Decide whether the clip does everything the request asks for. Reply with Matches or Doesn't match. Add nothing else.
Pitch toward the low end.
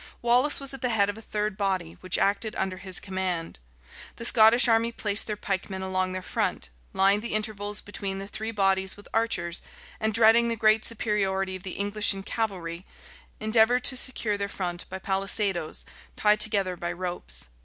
Doesn't match